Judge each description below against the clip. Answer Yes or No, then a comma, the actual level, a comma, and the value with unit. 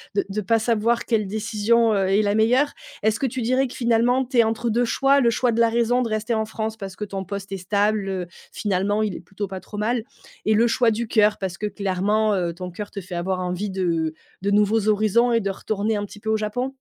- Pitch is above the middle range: Yes, high, 215 Hz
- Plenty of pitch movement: No, average, 2.7 semitones